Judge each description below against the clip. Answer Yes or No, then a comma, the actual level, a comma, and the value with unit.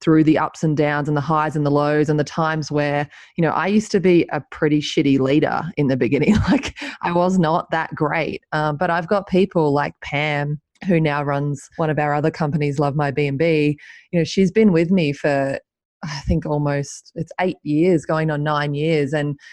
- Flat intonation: Yes, narrow, 2.1 semitones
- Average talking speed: No, fast, 215 wpm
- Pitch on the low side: No, medium, 150 Hz